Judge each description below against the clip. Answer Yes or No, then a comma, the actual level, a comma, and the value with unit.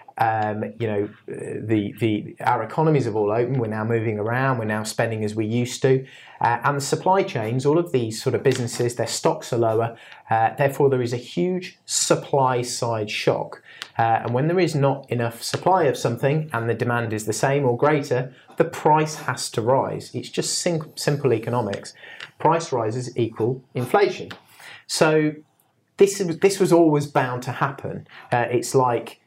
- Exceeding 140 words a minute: Yes, average, 180 wpm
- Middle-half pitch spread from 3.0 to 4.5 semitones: Yes, average, 4.2 semitones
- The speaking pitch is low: Yes, low, 125 Hz